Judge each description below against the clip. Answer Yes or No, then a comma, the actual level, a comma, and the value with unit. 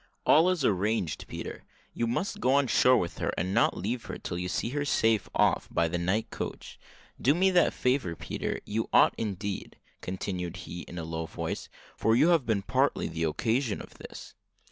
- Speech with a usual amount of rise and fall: No, wide, 6.3 semitones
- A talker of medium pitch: No, low, 110 Hz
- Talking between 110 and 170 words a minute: No, average, 195 wpm